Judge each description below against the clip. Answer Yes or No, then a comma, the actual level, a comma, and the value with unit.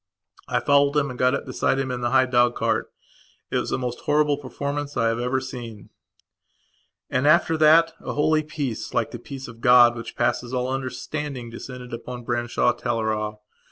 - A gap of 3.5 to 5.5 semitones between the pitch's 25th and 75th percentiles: No, average, 2.9 semitones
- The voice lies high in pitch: No, low, 125 Hz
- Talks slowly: No, average, 185 wpm